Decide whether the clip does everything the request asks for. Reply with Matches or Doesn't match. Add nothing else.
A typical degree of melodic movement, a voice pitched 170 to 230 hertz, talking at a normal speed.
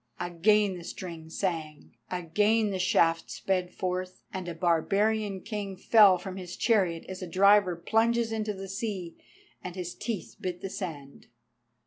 Matches